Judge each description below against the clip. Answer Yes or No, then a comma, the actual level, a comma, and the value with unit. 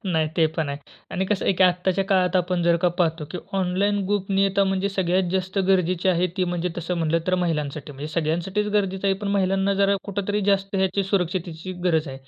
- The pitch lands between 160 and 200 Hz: Yes, medium, 185 Hz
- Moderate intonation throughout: No, narrow, 2.3 semitones